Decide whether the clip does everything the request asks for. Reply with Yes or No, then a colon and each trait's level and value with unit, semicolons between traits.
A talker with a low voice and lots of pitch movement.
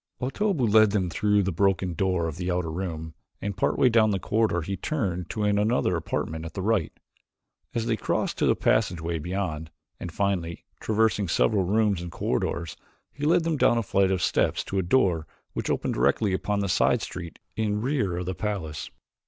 No: very low, 95 Hz; average, 3.8 semitones